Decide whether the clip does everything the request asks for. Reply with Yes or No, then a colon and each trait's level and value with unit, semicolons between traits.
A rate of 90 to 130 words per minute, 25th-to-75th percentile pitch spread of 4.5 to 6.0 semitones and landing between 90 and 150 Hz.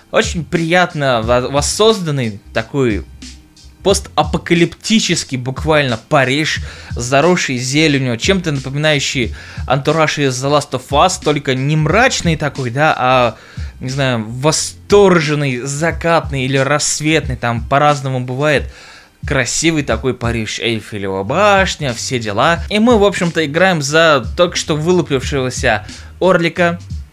Yes: slow, 110 wpm; average, 5.1 semitones; medium, 140 Hz